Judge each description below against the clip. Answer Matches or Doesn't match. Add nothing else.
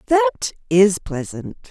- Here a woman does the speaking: Matches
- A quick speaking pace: Doesn't match